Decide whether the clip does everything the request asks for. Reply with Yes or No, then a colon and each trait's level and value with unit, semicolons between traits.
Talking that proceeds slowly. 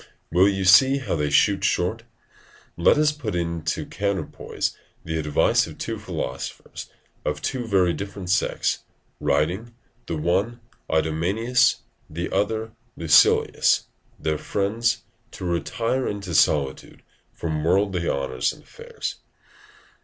Yes: slow, 130 wpm